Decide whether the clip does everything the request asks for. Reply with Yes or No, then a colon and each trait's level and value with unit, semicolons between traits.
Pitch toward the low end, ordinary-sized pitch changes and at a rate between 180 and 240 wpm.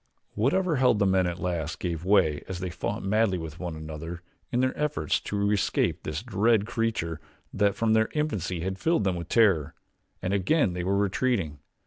Yes: very low, 95 Hz; average, 4.6 semitones; average, 185 wpm